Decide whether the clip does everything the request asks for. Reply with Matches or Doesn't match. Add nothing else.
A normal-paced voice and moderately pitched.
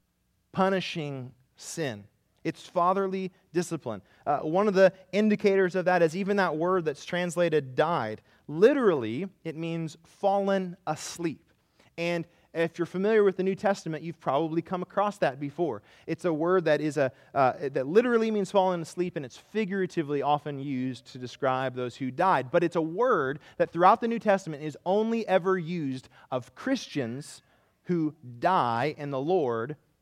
Matches